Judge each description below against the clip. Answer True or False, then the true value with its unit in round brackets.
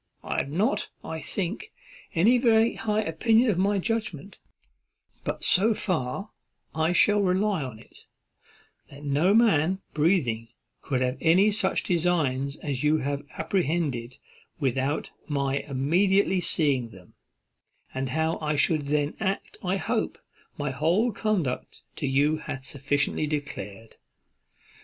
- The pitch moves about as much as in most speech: False (5.7 semitones)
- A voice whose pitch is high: False (160 Hz)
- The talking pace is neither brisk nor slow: False (130 wpm)